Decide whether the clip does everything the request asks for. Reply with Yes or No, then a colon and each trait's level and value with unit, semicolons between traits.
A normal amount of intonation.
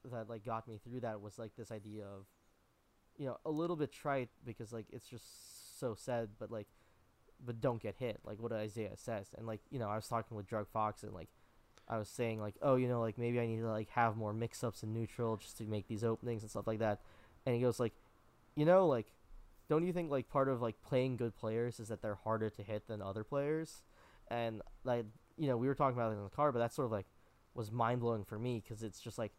No: narrow, 2.2 semitones